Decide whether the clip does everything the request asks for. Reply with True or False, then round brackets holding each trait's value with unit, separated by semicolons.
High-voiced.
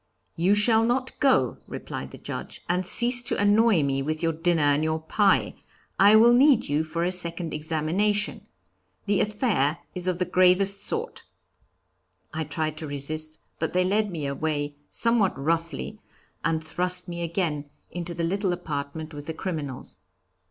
False (170 Hz)